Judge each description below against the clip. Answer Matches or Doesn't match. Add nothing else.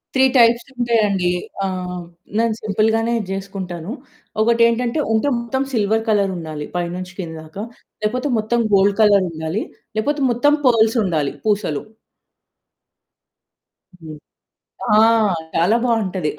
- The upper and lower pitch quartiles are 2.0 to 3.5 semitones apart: Doesn't match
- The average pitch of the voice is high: Matches